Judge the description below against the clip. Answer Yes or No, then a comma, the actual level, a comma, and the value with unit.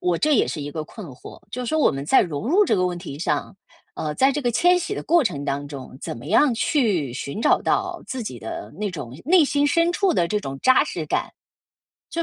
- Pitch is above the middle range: Yes, high, 210 Hz